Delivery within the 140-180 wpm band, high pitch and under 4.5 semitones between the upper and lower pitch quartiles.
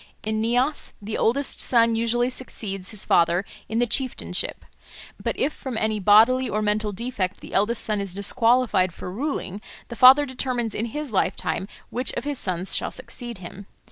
Yes: average, 175 wpm; high, 225 Hz; average, 3.9 semitones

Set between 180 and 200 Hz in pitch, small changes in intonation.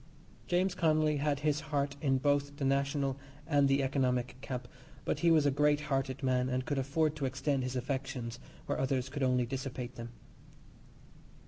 No: medium, 140 Hz; narrow, 2.1 semitones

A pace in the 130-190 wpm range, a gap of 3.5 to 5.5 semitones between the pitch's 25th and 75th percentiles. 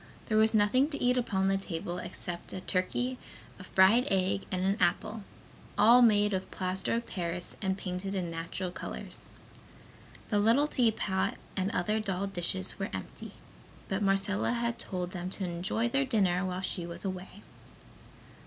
No: average, 165 wpm; average, 3.1 semitones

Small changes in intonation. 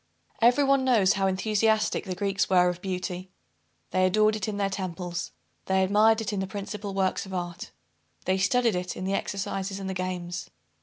Yes: narrow, 2.2 semitones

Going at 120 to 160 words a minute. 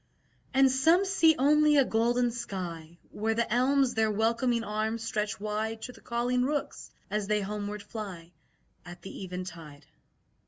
Yes: average, 150 wpm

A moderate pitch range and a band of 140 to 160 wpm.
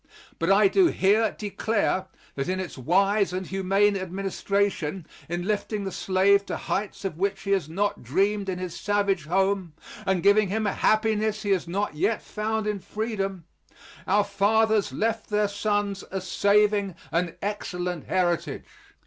No: narrow, 1.9 semitones; average, 155 wpm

